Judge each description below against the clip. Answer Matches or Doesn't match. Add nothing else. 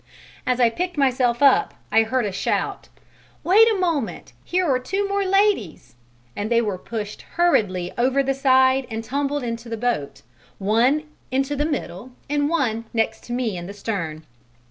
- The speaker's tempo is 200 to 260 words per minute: Doesn't match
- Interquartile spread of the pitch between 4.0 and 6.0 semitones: Matches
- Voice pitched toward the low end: Doesn't match